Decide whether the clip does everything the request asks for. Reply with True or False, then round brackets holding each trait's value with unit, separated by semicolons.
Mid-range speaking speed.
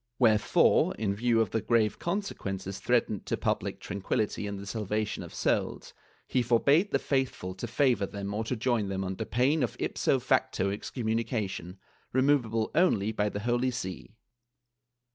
True (155 wpm)